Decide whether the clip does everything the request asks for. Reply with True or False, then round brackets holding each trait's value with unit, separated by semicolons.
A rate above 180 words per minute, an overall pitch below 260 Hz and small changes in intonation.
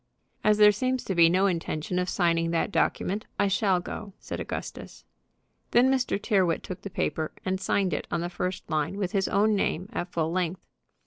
False (195 wpm; 185 Hz; 3.0 semitones)